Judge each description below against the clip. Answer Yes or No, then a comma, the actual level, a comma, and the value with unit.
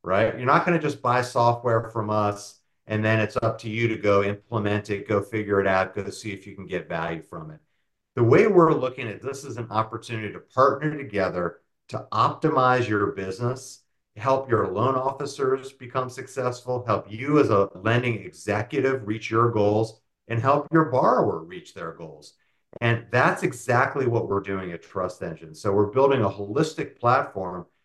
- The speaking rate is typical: Yes, average, 185 wpm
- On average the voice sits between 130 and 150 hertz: No, low, 110 Hz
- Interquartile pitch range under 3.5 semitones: No, average, 4.3 semitones